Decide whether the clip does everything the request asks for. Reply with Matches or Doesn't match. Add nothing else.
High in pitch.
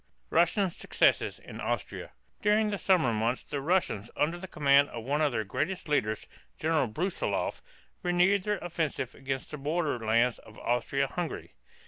Doesn't match